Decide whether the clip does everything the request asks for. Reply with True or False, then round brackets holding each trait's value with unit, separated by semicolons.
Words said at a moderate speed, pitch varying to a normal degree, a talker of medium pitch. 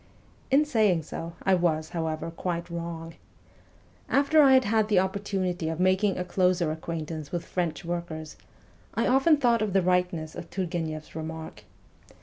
True (155 wpm; 3.6 semitones; 175 Hz)